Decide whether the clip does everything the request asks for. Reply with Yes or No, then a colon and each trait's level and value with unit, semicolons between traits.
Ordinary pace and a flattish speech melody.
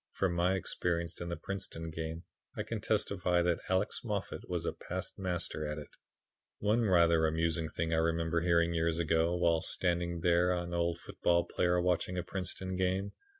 Yes: average, 175 wpm; narrow, 1.6 semitones